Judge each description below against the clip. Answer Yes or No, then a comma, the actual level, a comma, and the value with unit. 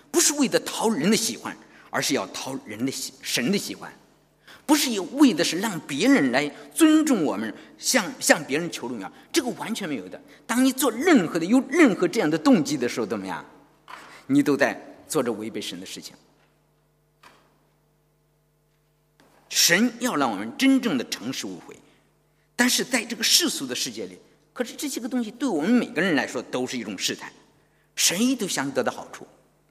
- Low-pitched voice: No, very high, 250 Hz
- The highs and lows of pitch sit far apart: Yes, wide, 7.9 semitones